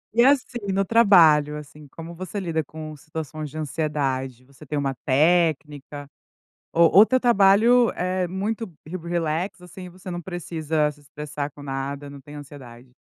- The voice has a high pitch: No, medium, 155 Hz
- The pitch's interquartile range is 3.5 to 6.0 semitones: Yes, average, 4.2 semitones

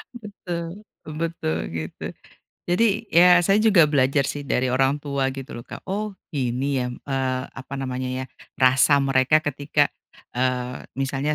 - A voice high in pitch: No, medium, 140 Hz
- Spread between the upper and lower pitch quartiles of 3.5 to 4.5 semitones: Yes, average, 4.0 semitones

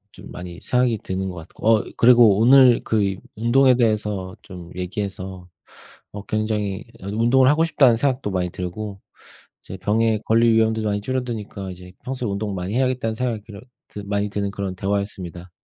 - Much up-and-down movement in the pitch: No, average, 3.4 semitones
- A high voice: No, low, 105 Hz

